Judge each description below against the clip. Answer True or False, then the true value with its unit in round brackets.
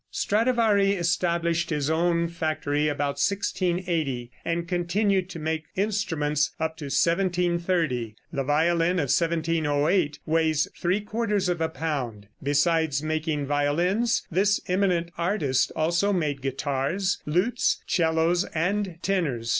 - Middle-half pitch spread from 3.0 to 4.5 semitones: True (3.6 semitones)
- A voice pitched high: False (165 Hz)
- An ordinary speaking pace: False (120 wpm)